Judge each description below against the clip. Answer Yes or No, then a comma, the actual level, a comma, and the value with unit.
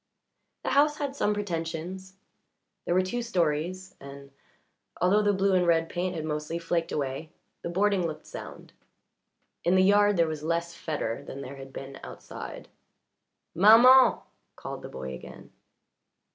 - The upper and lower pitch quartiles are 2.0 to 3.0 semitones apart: No, average, 4.3 semitones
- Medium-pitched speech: Yes, medium, 170 Hz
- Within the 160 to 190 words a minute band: No, average, 150 wpm